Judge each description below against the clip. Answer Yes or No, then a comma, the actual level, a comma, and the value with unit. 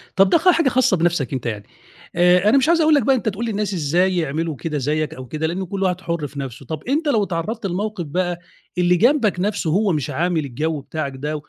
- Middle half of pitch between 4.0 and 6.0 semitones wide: Yes, wide, 5.4 semitones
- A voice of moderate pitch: Yes, medium, 175 Hz